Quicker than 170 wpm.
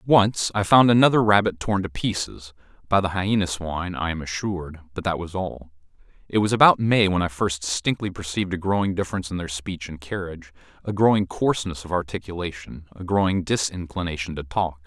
Yes: average, 180 wpm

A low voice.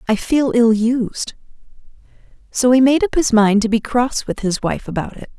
No: high, 235 Hz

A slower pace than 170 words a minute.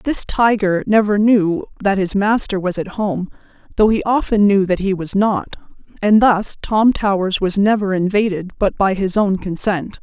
No: average, 180 wpm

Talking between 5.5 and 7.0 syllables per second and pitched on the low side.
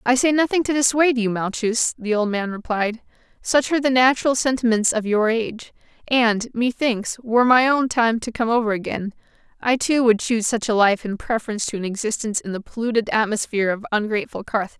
No: 6.0 syllables/s; high, 230 Hz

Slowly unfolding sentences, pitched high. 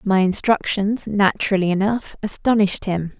Yes: slow, 115 wpm; high, 200 Hz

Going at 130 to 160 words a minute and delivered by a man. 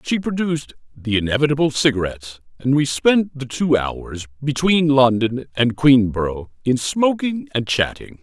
Yes: average, 140 wpm; male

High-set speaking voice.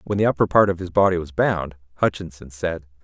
No: very low, 90 Hz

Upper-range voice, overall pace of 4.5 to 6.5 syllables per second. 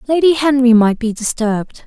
Yes: very high, 250 Hz; 5.3 syllables/s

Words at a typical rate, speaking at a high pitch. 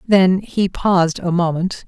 No: average, 160 wpm; medium, 180 Hz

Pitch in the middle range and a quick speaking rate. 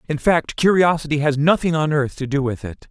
Yes: medium, 150 Hz; fast, 225 wpm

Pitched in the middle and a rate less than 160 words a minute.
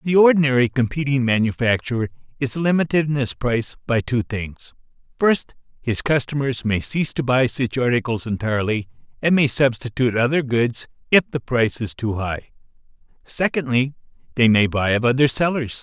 No: low, 130 Hz; average, 150 wpm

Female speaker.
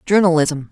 Yes: female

